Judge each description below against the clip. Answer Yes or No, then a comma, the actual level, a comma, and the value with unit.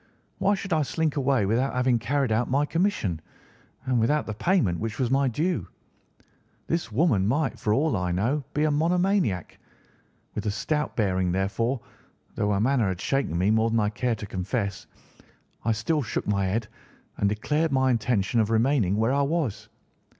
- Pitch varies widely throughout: Yes, wide, 5.8 semitones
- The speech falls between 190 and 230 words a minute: No, average, 180 wpm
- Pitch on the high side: No, low, 120 Hz